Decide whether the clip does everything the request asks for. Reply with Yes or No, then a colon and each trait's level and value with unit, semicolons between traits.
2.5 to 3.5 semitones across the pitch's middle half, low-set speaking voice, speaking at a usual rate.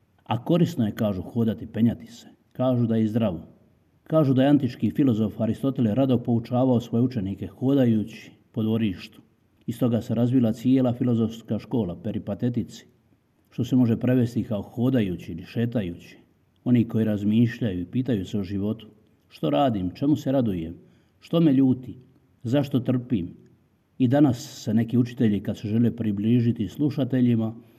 Yes: average, 2.8 semitones; low, 115 Hz; average, 145 wpm